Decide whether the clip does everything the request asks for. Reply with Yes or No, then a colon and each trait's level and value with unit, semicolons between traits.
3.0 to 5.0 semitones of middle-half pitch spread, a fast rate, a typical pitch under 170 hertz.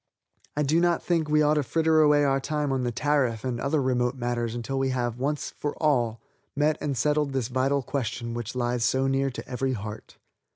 Yes: average, 3.3 semitones; fast, 210 wpm; low, 135 Hz